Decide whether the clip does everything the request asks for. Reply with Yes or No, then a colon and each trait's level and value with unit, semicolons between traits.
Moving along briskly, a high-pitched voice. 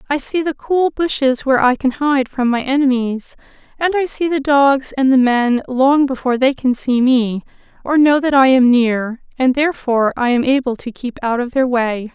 Yes: fast, 210 wpm; very high, 260 Hz